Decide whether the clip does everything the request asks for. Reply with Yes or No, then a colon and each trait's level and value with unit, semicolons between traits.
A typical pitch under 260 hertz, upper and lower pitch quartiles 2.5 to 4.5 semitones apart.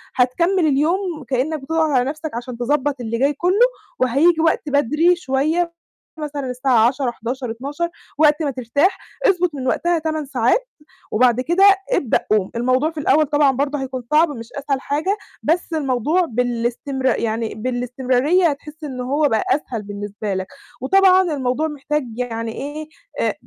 No: very high, 280 Hz; average, 4.0 semitones